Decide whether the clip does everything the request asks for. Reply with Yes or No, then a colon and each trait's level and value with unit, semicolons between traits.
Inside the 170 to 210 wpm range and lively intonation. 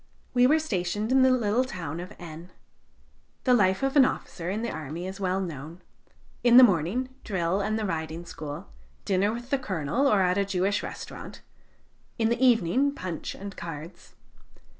Yes: average, 175 wpm; wide, 5.8 semitones